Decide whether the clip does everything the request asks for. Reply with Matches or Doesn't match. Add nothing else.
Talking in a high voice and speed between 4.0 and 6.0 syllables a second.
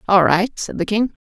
Matches